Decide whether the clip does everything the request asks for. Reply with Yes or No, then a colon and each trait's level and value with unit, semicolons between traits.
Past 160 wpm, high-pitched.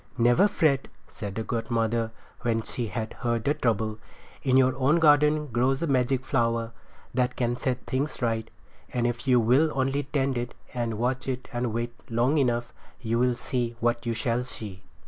No: average, 180 wpm; low, 120 Hz